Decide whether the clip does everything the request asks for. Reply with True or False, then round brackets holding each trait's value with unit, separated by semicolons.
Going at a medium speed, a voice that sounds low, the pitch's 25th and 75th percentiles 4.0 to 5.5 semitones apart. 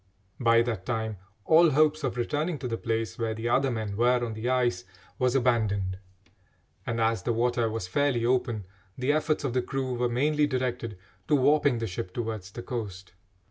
False (185 wpm; 120 Hz; 2.7 semitones)